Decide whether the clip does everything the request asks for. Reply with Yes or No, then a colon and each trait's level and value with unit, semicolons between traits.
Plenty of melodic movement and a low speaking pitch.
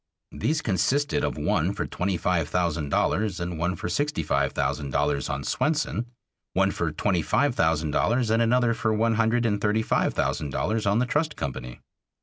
Yes: wide, 6.4 semitones; low, 100 Hz